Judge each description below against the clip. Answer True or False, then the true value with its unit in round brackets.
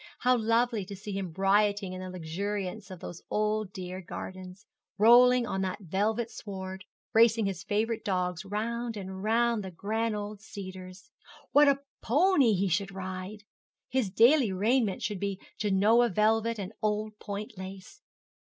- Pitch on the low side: False (205 Hz)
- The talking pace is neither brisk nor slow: True (155 wpm)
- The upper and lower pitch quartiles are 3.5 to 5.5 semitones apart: False (3.0 semitones)